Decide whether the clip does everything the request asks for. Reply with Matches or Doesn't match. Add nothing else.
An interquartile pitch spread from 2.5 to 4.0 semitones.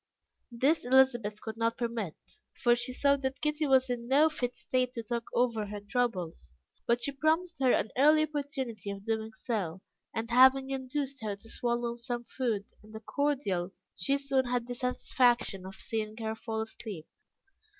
Matches